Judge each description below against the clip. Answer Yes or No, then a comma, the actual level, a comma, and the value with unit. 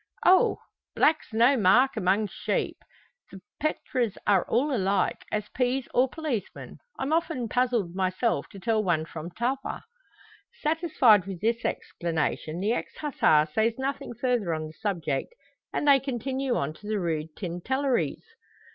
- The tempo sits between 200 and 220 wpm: No, average, 145 wpm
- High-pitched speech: Yes, high, 225 Hz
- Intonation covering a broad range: Yes, wide, 6.3 semitones